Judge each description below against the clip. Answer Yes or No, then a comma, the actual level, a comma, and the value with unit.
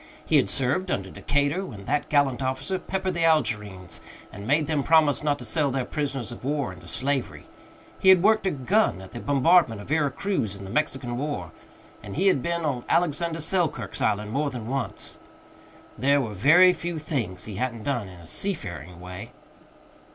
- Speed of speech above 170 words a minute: Yes, average, 190 wpm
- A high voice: No, medium, 140 Hz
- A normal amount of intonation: No, wide, 6.4 semitones